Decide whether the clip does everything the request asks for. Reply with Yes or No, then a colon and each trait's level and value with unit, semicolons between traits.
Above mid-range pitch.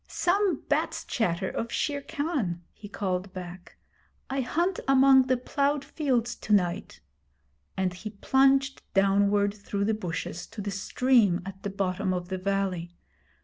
Yes: high, 205 Hz